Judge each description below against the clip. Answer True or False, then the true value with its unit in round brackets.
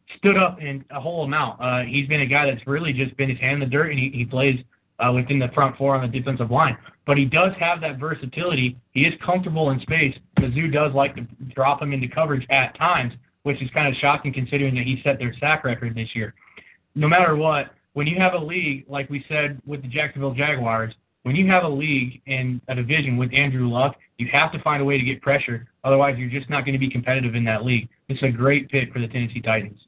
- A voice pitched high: False (135 Hz)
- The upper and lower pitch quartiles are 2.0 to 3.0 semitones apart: True (2.7 semitones)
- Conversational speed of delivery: False (245 wpm)